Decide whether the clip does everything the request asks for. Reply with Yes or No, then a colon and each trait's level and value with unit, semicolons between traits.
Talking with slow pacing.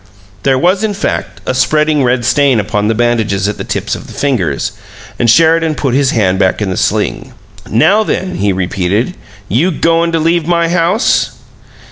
No: average, 180 wpm